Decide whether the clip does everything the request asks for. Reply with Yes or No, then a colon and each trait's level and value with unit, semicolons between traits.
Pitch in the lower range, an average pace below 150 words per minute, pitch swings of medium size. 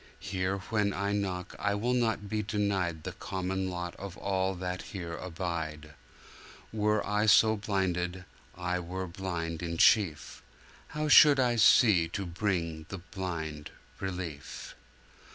Yes: very low, 95 Hz; slow, 135 wpm; average, 3.0 semitones